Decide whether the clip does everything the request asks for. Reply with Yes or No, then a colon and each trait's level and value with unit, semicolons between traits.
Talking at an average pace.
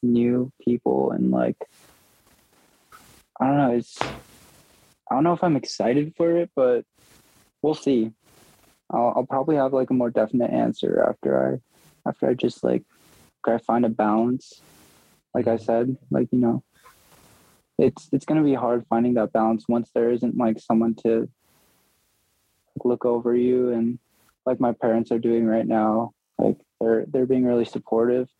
Yes: average, 165 wpm